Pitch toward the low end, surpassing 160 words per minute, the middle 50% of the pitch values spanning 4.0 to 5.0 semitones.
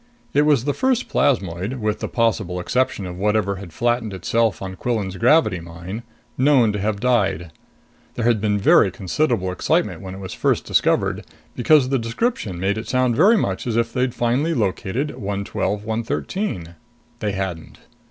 Yes: low, 110 Hz; average, 170 wpm; average, 4.7 semitones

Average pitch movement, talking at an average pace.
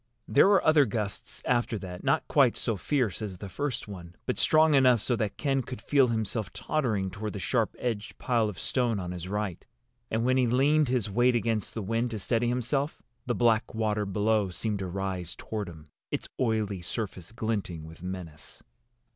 Yes: average, 4.1 semitones; average, 190 wpm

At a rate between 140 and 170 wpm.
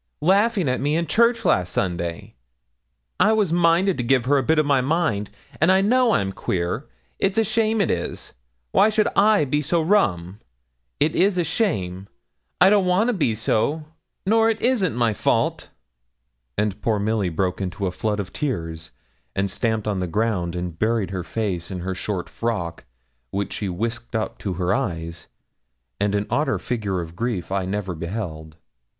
No: average, 180 wpm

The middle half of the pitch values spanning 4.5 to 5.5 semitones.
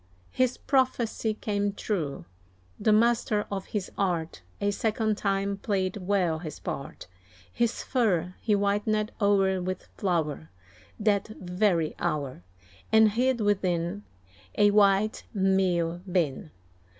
No: average, 3.1 semitones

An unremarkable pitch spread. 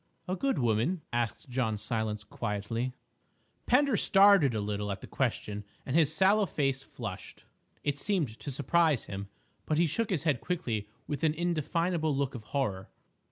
No: wide, 7.4 semitones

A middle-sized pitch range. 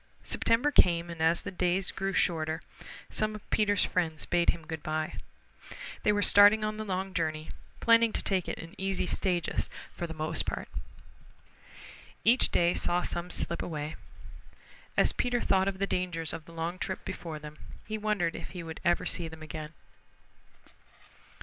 Yes: average, 3.4 semitones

